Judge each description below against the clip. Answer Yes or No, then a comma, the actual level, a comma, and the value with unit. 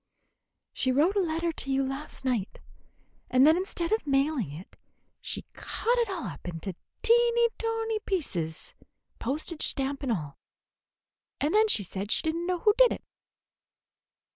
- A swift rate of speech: No, average, 155 wpm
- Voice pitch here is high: Yes, very high, 305 Hz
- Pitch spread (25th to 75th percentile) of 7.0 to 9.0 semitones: Yes, wide, 7.7 semitones